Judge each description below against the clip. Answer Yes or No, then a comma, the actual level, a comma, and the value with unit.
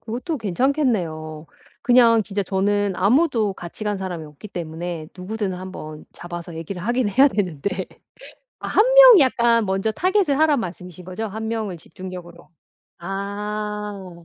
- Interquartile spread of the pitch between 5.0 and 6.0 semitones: No, average, 4.5 semitones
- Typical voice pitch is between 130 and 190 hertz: No, high, 200 Hz